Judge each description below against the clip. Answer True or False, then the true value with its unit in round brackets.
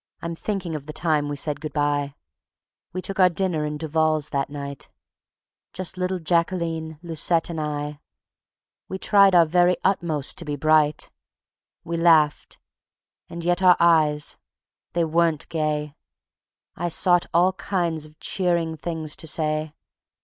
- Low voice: False (160 Hz)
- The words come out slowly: False (150 wpm)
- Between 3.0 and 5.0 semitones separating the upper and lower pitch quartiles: False (2.4 semitones)